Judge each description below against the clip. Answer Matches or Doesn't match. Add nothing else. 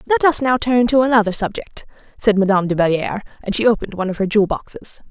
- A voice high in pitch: Matches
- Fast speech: Matches